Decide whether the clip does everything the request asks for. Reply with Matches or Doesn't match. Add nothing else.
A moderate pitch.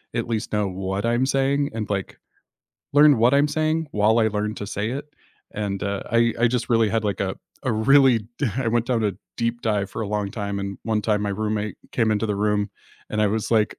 Doesn't match